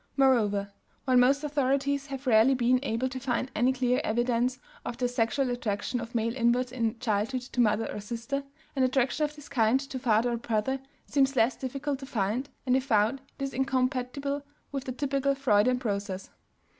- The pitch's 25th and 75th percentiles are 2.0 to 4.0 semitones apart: Yes, average, 2.8 semitones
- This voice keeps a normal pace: Yes, average, 180 wpm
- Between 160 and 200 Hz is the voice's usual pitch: No, very high, 255 Hz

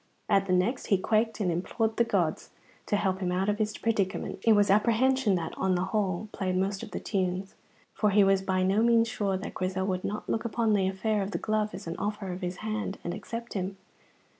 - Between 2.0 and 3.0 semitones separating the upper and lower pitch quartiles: Yes, narrow, 2.5 semitones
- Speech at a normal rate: No, fast, 230 wpm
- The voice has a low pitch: No, high, 200 Hz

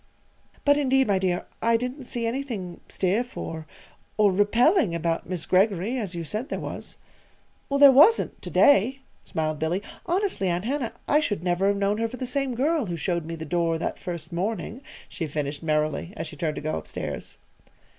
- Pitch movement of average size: No, wide, 7.0 semitones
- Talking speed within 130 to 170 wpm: No, average, 190 wpm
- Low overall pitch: No, high, 200 Hz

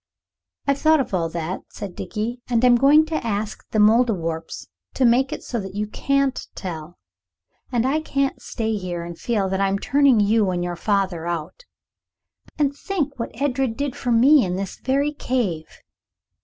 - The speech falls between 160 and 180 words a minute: Yes, average, 170 wpm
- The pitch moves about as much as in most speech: No, wide, 6.4 semitones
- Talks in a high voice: Yes, high, 230 Hz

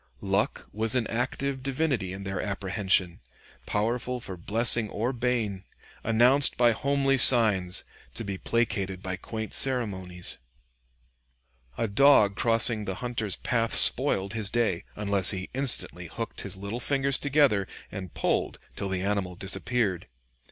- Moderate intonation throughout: Yes, average, 4.1 semitones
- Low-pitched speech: Yes, low, 110 Hz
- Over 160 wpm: No, slow, 135 wpm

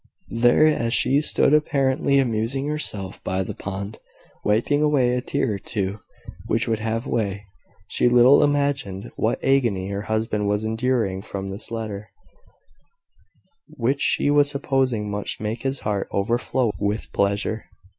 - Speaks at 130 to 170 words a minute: Yes, average, 145 wpm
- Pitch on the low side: Yes, low, 115 Hz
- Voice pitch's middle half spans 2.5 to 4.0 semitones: No, average, 4.7 semitones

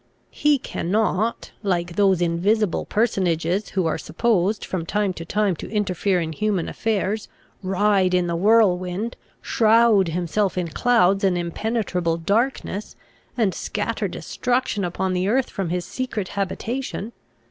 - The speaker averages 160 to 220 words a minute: No, slow, 135 wpm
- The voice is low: No, high, 195 Hz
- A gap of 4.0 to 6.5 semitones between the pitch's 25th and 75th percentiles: No, average, 3.5 semitones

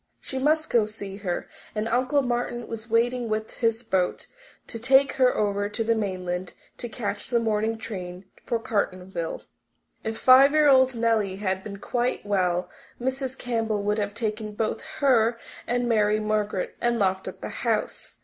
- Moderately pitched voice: No, high, 220 Hz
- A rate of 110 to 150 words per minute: No, average, 170 wpm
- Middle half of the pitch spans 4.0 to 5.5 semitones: No, average, 3.1 semitones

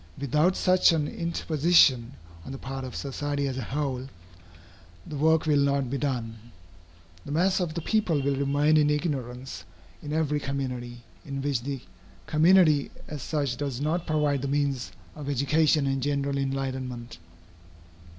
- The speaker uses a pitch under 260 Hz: Yes, medium, 140 Hz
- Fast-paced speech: No, average, 150 wpm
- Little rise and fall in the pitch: Yes, narrow, 2.3 semitones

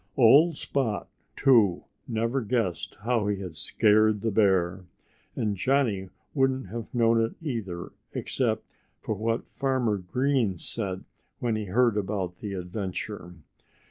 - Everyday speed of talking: No, slow, 130 wpm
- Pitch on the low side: Yes, low, 110 Hz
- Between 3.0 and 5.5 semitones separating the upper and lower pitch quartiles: Yes, average, 4.1 semitones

